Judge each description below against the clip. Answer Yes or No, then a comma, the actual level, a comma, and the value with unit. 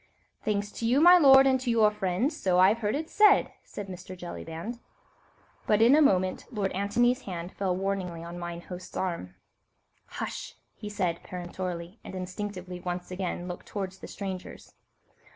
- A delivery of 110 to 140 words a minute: No, average, 165 wpm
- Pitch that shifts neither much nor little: Yes, average, 3.6 semitones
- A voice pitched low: No, high, 190 Hz